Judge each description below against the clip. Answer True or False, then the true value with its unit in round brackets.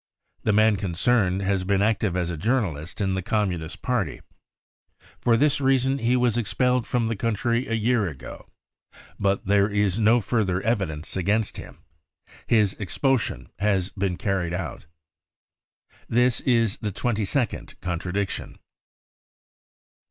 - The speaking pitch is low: True (105 Hz)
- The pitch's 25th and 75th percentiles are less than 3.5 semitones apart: False (3.9 semitones)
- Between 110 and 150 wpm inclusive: True (135 wpm)